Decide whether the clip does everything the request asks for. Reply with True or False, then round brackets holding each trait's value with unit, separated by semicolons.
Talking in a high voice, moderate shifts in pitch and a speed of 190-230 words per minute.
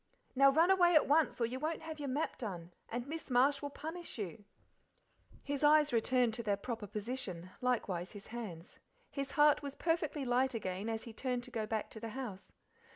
True (250 Hz; 5.0 semitones; 200 wpm)